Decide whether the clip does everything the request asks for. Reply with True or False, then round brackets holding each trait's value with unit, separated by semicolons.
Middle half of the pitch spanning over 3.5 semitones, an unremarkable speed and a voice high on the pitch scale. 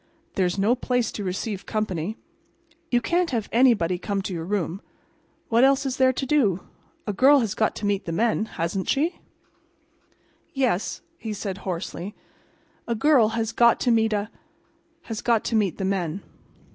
True (4.1 semitones; 165 wpm; 215 Hz)